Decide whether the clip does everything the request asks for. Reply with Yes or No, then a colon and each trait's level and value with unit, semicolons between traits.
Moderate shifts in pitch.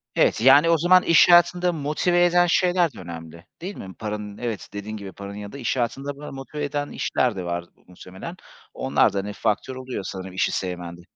No: wide, 8.1 semitones